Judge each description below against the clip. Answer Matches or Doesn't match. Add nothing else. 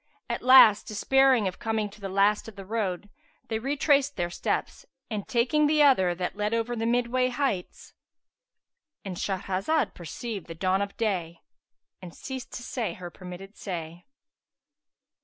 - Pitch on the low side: Doesn't match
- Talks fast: Doesn't match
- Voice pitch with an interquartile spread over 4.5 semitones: Matches